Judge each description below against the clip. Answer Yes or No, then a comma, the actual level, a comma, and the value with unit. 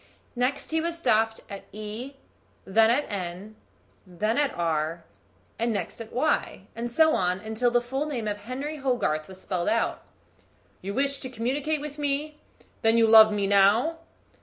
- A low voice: No, high, 230 Hz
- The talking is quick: No, average, 165 wpm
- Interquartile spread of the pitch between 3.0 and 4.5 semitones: No, wide, 5.4 semitones